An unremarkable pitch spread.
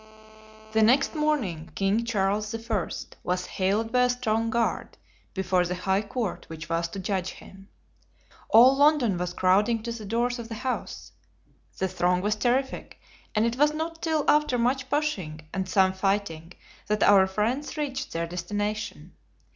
Yes: average, 4.7 semitones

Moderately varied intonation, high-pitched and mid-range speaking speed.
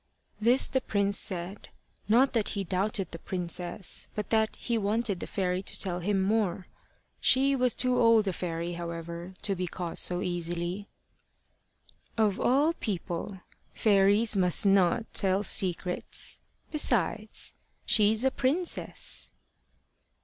No: average, 3.8 semitones; high, 200 Hz; slow, 130 wpm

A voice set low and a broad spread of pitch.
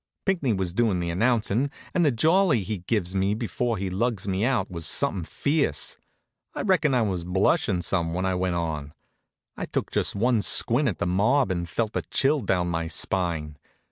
Yes: low, 100 Hz; wide, 5.7 semitones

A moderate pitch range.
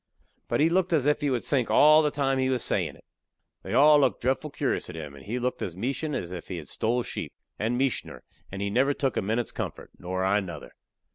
No: wide, 6.6 semitones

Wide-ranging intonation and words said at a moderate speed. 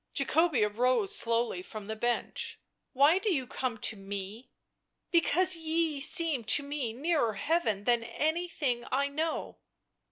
Yes: wide, 6.0 semitones; average, 165 wpm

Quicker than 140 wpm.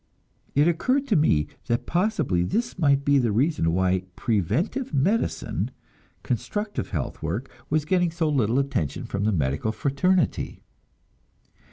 No: slow, 135 wpm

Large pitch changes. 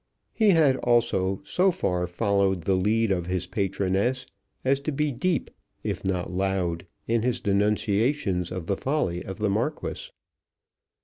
Yes: wide, 5.7 semitones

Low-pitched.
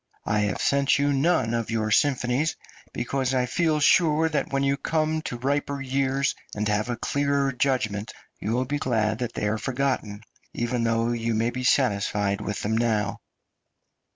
Yes: low, 125 Hz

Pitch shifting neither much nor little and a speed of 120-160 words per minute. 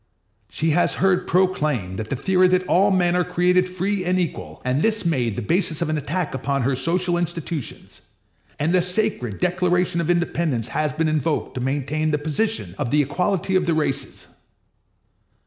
No: average, 4.2 semitones; average, 175 wpm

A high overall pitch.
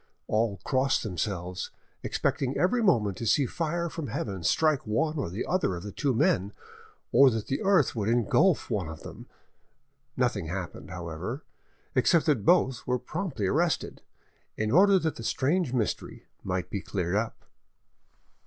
No: low, 120 Hz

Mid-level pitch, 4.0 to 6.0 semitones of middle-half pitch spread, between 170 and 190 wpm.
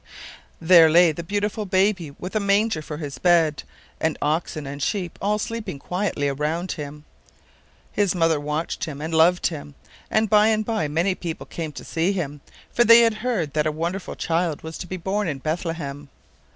Yes: medium, 170 Hz; average, 4.5 semitones; average, 185 wpm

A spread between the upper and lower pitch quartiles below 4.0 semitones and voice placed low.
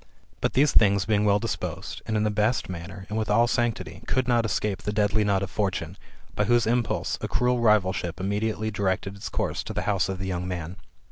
Yes: narrow, 2.6 semitones; low, 105 Hz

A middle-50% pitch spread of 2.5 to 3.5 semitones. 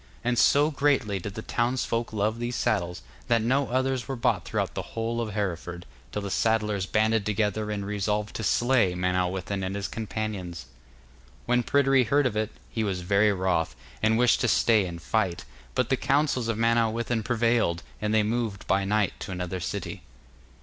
Yes: average, 3.2 semitones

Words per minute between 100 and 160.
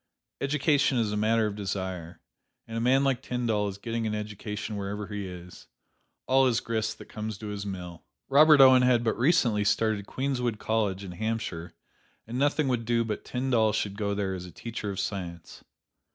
No: average, 185 wpm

